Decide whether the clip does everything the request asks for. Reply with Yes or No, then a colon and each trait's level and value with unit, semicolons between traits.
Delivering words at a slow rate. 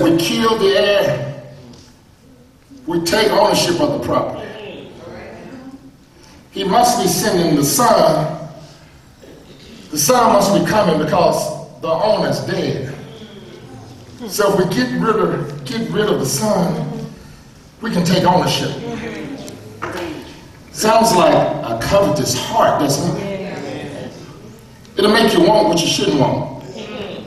Yes: slow, 120 wpm